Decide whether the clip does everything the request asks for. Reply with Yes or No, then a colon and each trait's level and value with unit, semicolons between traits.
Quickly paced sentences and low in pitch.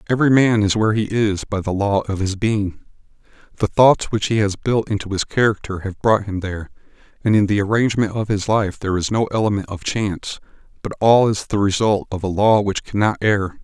Yes: fast, 215 wpm; low, 105 Hz